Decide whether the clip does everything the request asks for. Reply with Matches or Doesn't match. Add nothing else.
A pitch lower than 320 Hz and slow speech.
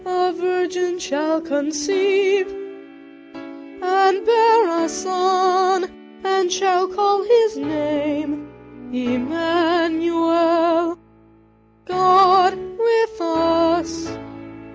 Doesn't match